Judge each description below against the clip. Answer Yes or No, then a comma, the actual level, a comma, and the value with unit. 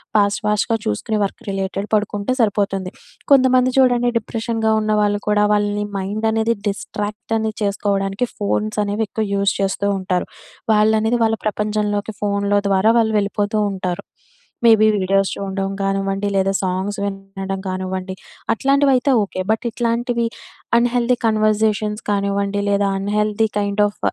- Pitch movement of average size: No, narrow, 2.0 semitones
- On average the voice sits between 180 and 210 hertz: Yes, high, 205 Hz